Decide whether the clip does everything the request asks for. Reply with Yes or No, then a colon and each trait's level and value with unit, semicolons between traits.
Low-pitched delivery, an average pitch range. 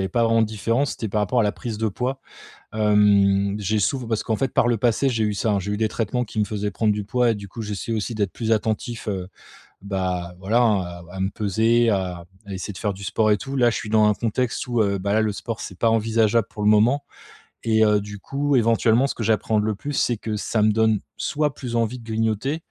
No: low, 110 Hz; narrow, 2.2 semitones